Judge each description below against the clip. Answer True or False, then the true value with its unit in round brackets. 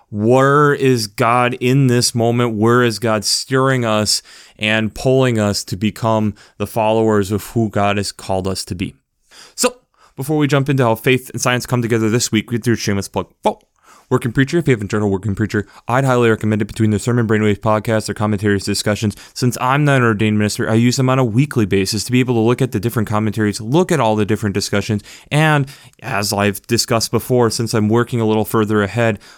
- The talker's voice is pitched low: True (115 Hz)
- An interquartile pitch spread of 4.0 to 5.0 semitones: False (3.0 semitones)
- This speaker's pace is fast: True (215 wpm)